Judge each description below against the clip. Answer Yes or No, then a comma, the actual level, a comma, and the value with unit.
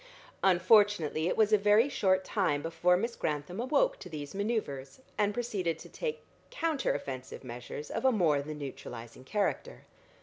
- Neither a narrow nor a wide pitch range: No, wide, 6.9 semitones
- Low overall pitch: No, medium, 185 Hz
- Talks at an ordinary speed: Yes, average, 160 wpm